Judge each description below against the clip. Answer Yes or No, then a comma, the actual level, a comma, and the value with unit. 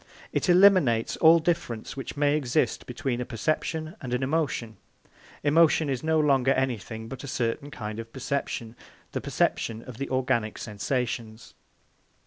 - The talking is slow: No, average, 145 wpm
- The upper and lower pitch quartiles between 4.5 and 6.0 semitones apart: Yes, average, 4.8 semitones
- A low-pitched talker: Yes, low, 130 Hz